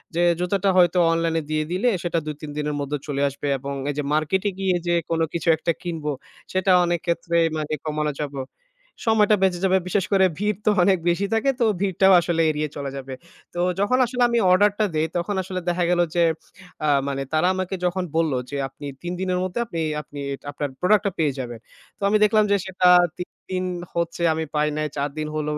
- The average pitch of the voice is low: No, medium, 175 Hz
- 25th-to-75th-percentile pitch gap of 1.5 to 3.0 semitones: No, average, 3.8 semitones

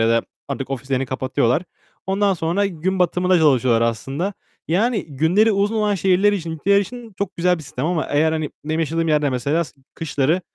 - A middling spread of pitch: No, wide, 5.7 semitones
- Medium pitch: Yes, medium, 165 Hz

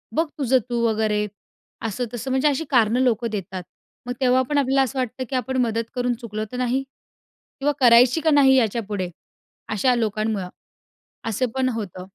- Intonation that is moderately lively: Yes, average, 3.2 semitones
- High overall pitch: Yes, high, 245 Hz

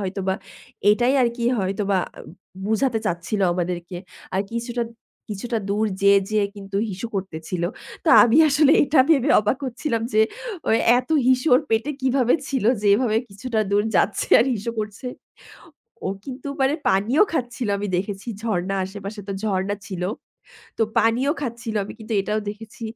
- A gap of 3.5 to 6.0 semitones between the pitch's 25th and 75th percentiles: Yes, average, 3.8 semitones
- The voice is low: No, high, 220 Hz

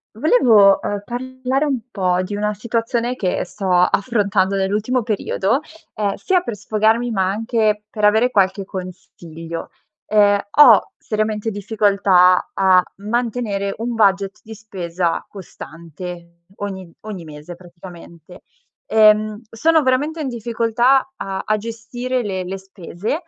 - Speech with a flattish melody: No, average, 3.6 semitones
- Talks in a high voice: Yes, high, 210 Hz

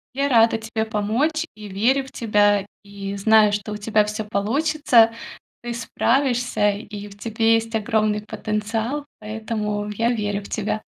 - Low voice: No, high, 220 Hz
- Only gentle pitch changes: Yes, narrow, 1.9 semitones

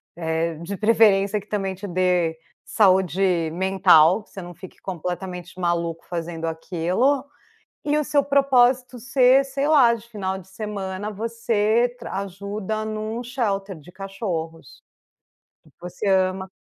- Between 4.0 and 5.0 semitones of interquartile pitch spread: Yes, average, 4.3 semitones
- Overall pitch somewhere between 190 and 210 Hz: Yes, high, 195 Hz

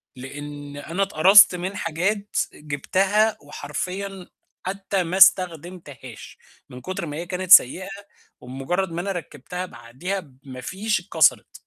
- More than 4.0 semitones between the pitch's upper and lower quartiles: Yes, average, 5.0 semitones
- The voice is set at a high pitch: No, medium, 175 Hz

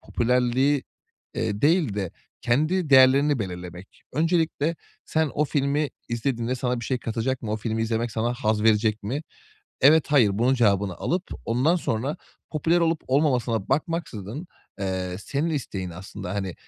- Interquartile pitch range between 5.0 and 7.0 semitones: Yes, average, 5.3 semitones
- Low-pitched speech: Yes, low, 125 Hz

